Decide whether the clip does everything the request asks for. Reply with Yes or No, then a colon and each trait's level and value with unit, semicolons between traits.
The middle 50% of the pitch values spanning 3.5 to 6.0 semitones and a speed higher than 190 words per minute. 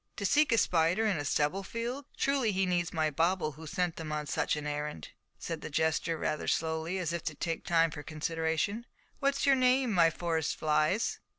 Yes: average, 4.4 semitones; average, 200 wpm